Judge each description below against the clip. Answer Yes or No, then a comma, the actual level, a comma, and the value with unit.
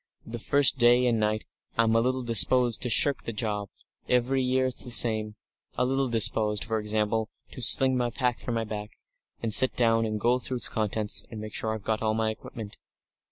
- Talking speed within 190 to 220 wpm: Yes, fast, 205 wpm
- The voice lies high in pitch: No, low, 115 Hz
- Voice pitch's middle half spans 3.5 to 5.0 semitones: No, narrow, 2.5 semitones